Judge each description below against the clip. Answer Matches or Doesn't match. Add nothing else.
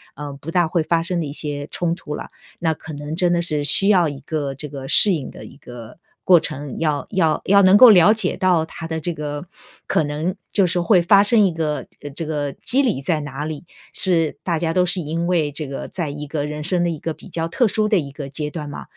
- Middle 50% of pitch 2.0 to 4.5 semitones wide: Matches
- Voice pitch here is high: Doesn't match